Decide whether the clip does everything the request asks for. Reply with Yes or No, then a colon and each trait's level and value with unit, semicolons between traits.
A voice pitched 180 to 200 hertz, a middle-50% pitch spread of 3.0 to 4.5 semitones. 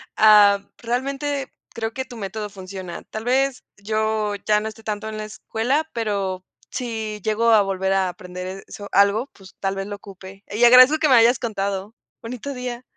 No: high, 215 Hz; average, 3.4 semitones